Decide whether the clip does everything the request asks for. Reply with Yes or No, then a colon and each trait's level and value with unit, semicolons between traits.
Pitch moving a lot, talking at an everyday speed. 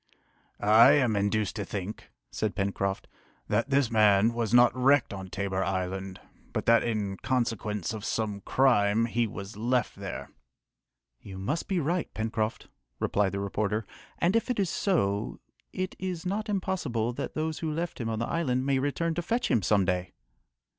Yes: wide, 6.1 semitones; average, 170 wpm